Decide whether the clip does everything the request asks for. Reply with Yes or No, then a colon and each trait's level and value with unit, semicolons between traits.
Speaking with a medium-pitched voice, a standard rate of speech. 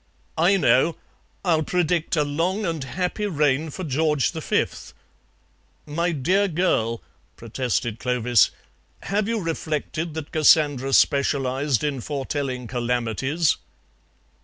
No: medium, 150 Hz; slow, 110 wpm